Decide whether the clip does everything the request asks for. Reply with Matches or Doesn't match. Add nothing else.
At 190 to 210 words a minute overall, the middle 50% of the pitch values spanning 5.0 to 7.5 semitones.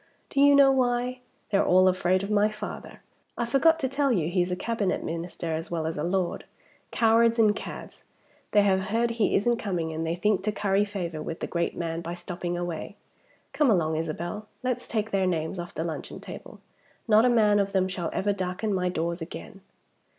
Doesn't match